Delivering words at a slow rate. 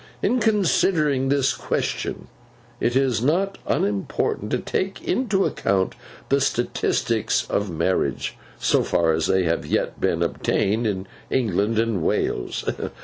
Yes: slow, 130 wpm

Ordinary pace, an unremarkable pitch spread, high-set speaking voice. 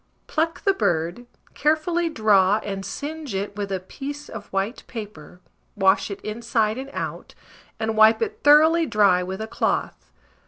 No: average, 155 wpm; wide, 7.2 semitones; high, 220 Hz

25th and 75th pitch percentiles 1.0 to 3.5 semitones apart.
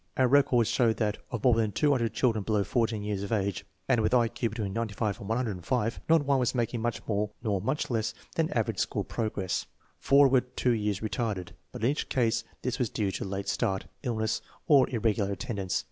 Yes: average, 3.2 semitones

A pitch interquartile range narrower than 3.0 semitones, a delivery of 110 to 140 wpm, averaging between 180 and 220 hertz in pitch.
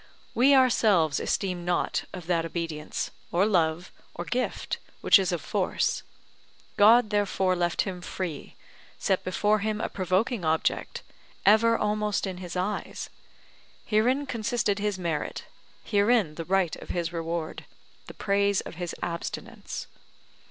No: average, 3.5 semitones; slow, 135 wpm; high, 190 Hz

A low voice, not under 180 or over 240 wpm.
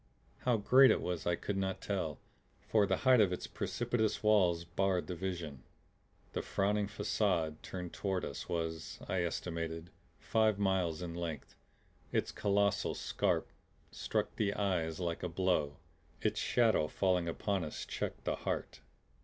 No: very low, 95 Hz; average, 150 wpm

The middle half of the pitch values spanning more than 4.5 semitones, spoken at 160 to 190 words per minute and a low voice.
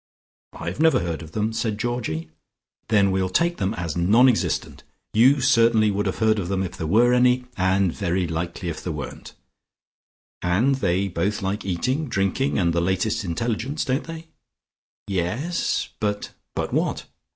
Yes: wide, 5.4 semitones; average, 165 wpm; low, 100 Hz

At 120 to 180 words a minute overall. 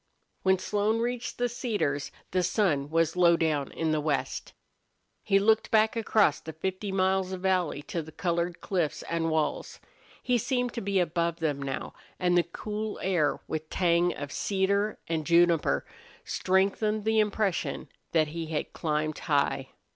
Yes: average, 160 wpm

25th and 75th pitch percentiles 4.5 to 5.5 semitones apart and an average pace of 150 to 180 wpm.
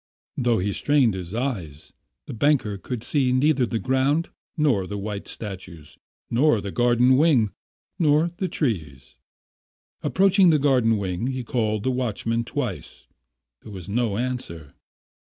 No: average, 5.1 semitones; average, 140 wpm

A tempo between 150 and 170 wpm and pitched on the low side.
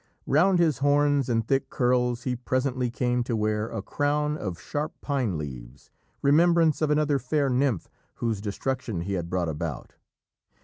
Yes: average, 160 wpm; low, 125 Hz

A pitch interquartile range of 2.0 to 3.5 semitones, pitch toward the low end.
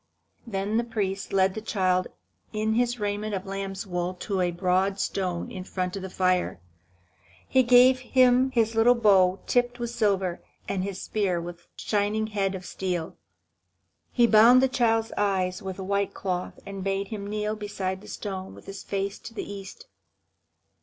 No: average, 2.7 semitones; high, 200 Hz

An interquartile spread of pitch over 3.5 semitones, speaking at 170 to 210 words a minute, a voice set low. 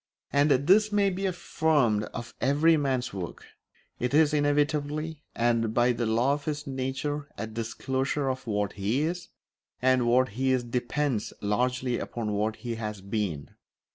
No: average, 4.4 semitones; average, 155 wpm; low, 130 Hz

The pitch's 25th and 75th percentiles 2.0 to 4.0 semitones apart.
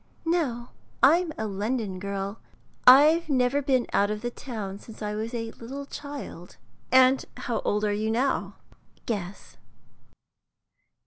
No: average, 4.5 semitones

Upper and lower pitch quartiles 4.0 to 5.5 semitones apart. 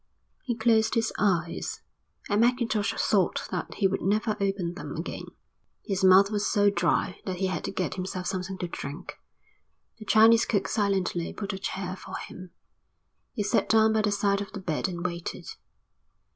No: narrow, 2.6 semitones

